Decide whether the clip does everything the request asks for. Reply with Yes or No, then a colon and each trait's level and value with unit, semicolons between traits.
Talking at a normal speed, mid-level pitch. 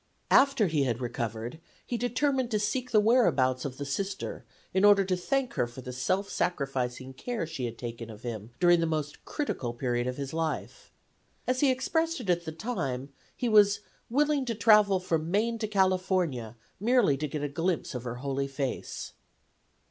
Yes: average, 185 wpm; medium, 170 Hz